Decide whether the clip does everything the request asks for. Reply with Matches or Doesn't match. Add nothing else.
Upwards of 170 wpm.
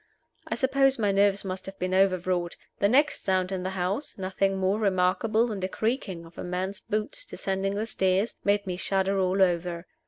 Matches